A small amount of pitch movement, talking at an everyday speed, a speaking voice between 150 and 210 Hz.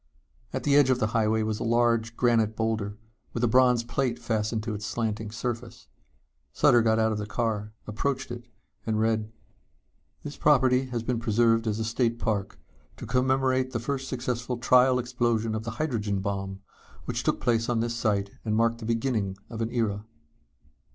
No: narrow, 2.1 semitones; average, 180 wpm; low, 115 Hz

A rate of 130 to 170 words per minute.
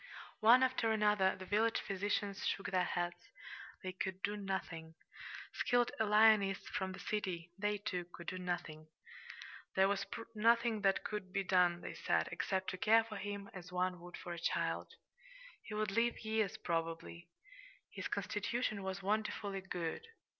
Yes: average, 155 wpm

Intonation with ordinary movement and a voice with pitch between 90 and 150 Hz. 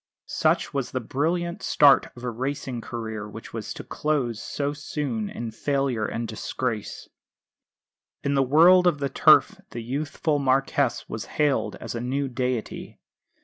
Yes: average, 3.5 semitones; low, 135 Hz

